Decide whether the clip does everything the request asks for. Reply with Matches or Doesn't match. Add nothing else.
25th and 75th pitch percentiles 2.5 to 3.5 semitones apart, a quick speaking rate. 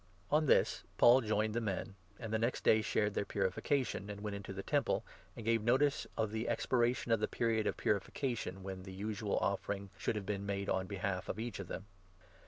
Matches